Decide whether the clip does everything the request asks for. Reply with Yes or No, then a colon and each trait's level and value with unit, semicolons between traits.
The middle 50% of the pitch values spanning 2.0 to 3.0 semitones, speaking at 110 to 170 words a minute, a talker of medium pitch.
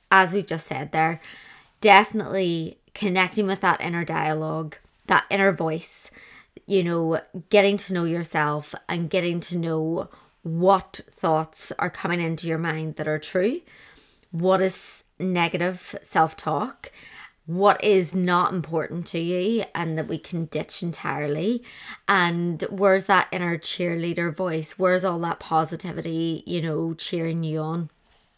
Yes: narrow, 2.6 semitones; average, 140 wpm; medium, 170 Hz